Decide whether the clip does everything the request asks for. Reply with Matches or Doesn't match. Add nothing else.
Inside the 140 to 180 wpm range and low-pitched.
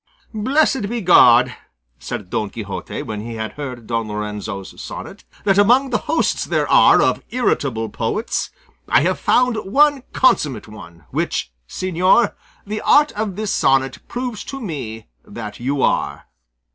Doesn't match